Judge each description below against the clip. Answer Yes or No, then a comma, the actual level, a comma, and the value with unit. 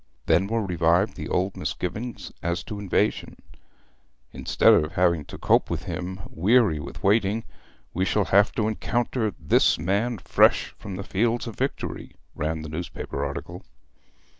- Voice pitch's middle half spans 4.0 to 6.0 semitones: Yes, average, 4.3 semitones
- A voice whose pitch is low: Yes, very low, 95 Hz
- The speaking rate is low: No, average, 150 wpm